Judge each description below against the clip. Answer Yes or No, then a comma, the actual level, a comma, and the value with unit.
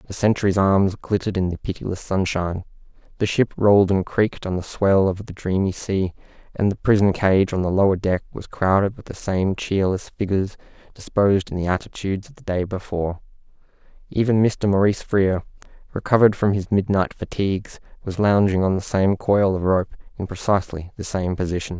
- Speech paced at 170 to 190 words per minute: Yes, average, 180 wpm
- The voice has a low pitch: Yes, very low, 95 Hz